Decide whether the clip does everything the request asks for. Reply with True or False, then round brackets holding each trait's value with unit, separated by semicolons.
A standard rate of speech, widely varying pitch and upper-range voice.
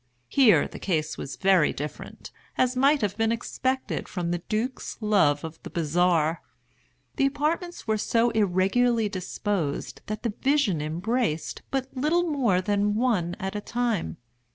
True (150 wpm; 6.1 semitones; 210 Hz)